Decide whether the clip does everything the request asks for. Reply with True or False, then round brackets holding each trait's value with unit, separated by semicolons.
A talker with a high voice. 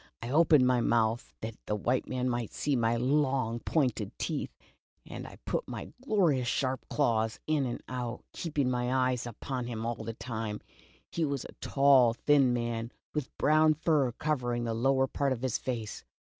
False (125 Hz)